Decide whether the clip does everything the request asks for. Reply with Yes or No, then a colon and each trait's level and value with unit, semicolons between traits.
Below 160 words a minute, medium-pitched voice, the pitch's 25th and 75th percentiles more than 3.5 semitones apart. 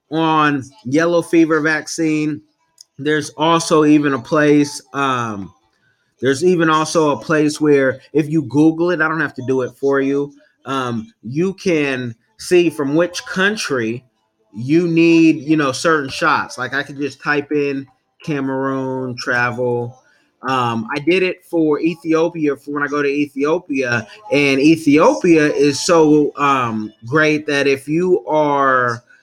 No: average, 145 wpm; medium, 145 Hz; average, 3.1 semitones